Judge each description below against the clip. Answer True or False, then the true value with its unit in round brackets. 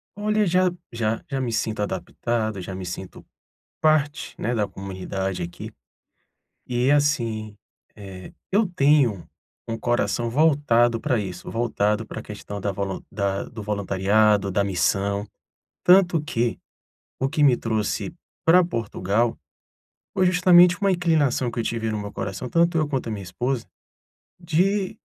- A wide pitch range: True (6.8 semitones)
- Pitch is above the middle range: False (115 Hz)